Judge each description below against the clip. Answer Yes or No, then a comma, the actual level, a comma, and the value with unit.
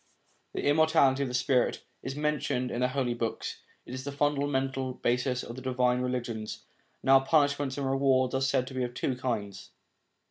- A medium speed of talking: Yes, average, 180 wpm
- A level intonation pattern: Yes, narrow, 1.8 semitones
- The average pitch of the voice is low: Yes, low, 130 Hz